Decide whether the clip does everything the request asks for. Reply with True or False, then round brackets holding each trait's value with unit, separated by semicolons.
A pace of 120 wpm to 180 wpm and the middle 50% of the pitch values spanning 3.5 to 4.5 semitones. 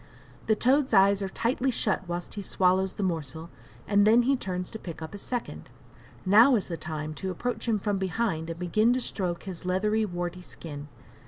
False (195 wpm; 3.9 semitones)